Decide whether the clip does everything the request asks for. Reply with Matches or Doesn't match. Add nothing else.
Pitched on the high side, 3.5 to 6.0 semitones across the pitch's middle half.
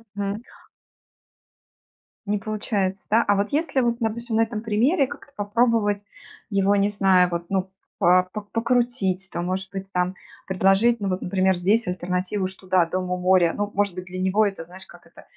Doesn't match